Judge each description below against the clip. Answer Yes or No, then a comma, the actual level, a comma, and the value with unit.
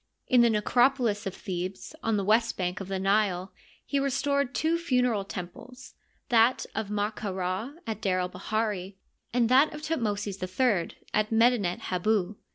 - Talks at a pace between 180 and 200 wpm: No, average, 165 wpm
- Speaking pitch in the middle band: No, high, 215 Hz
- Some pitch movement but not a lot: Yes, average, 4.5 semitones